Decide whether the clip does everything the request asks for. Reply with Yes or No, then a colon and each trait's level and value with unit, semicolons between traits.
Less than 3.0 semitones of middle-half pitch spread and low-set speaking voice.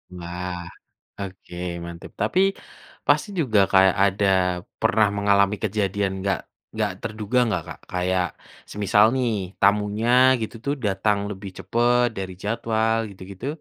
Yes: narrow, 2.5 semitones; low, 100 Hz